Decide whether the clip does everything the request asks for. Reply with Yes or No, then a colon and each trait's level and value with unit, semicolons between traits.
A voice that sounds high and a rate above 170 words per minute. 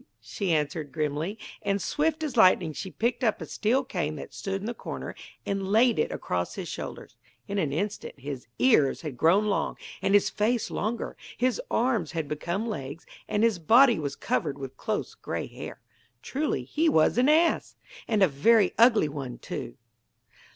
Yes: high, 200 Hz; average, 180 wpm